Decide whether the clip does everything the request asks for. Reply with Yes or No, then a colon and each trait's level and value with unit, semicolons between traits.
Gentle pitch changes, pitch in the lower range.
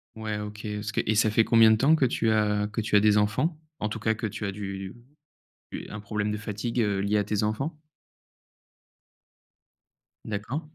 Yes: narrow, 1.3 semitones; low, 105 Hz